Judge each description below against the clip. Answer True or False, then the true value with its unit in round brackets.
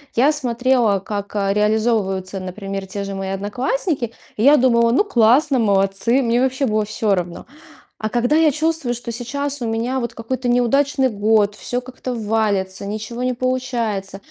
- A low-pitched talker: False (230 Hz)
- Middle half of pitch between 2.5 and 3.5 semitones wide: False (3.9 semitones)